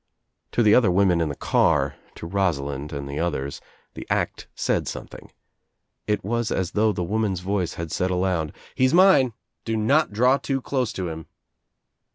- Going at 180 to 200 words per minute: Yes, average, 185 wpm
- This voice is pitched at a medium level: No, very low, 95 Hz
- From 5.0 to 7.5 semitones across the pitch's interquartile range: Yes, average, 5.3 semitones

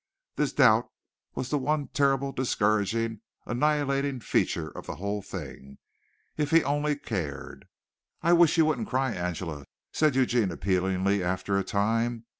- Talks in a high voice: No, low, 120 Hz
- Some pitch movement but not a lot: No, wide, 6.4 semitones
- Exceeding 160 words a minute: No, average, 140 wpm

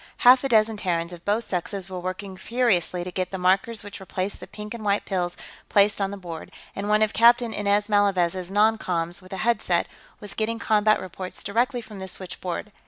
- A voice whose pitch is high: Yes, high, 200 Hz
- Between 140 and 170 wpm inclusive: No, fast, 205 wpm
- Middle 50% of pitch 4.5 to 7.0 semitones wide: No, average, 2.8 semitones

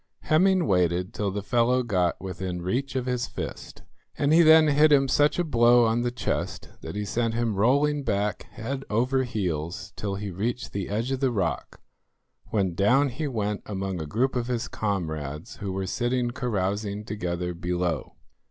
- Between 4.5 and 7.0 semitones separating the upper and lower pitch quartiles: Yes, average, 5.1 semitones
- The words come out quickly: No, average, 180 wpm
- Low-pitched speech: Yes, low, 110 Hz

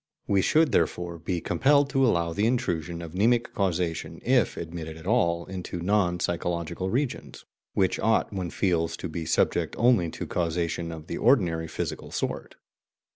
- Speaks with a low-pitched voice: Yes, very low, 90 Hz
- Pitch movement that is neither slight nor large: Yes, average, 4.0 semitones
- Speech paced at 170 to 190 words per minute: No, average, 160 wpm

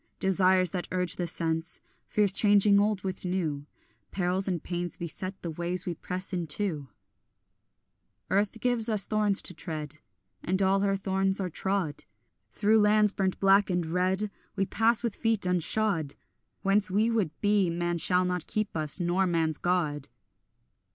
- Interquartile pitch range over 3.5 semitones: No, average, 2.8 semitones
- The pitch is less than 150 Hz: No, medium, 185 Hz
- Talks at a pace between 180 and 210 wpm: No, average, 155 wpm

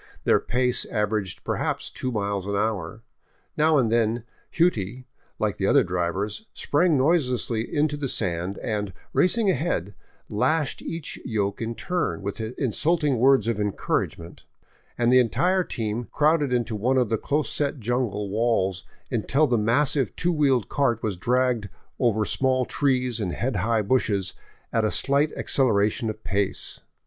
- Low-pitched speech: Yes, low, 120 Hz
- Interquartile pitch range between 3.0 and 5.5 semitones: Yes, average, 4.8 semitones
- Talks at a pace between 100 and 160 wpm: Yes, average, 155 wpm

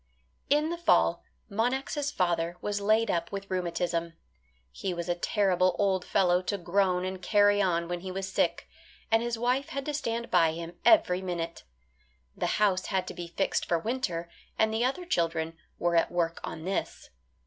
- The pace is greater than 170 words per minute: Yes, average, 180 wpm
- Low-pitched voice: No, high, 190 Hz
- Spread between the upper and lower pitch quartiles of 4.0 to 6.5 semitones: Yes, average, 4.3 semitones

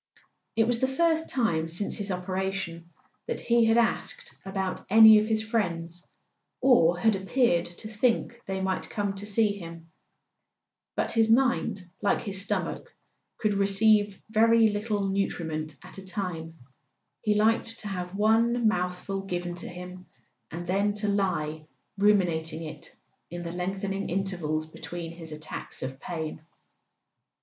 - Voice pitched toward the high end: Yes, high, 195 Hz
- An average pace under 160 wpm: Yes, average, 145 wpm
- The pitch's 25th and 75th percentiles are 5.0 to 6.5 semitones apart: No, average, 3.9 semitones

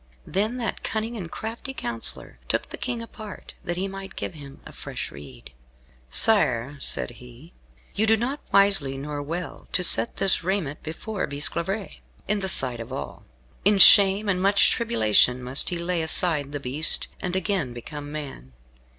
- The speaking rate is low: No, average, 165 wpm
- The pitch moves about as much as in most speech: No, wide, 6.7 semitones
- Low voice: No, medium, 170 Hz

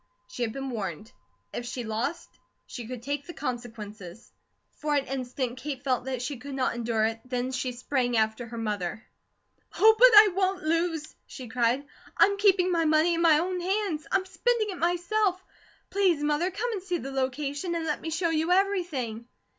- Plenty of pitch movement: Yes, wide, 6.5 semitones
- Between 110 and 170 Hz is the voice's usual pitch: No, very high, 285 Hz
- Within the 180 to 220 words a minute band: Yes, average, 185 wpm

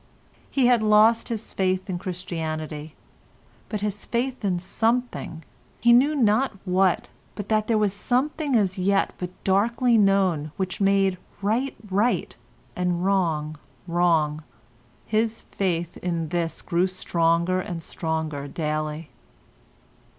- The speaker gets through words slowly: Yes, slow, 120 wpm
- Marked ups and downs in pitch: No, average, 4.5 semitones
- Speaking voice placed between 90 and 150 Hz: No, medium, 185 Hz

